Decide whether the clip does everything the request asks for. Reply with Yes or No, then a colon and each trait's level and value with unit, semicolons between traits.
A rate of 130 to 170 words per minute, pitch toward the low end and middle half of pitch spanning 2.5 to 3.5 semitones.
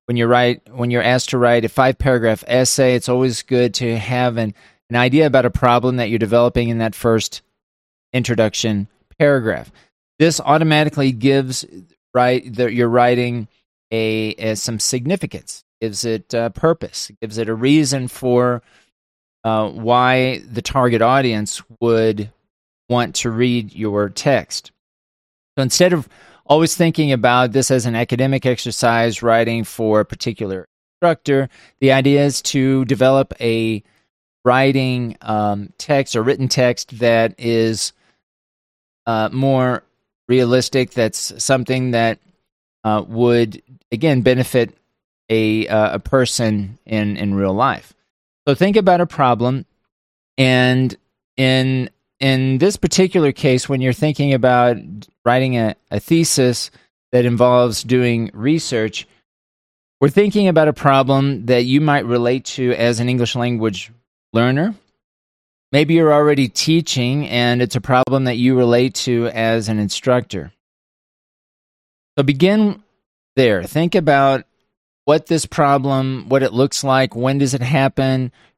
Yes: slow, 135 wpm; low, 125 Hz; average, 2.9 semitones